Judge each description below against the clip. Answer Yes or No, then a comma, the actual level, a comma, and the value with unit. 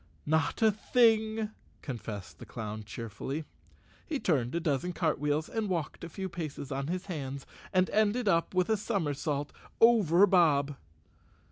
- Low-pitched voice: No, medium, 165 Hz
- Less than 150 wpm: Yes, average, 140 wpm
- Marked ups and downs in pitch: Yes, wide, 6.4 semitones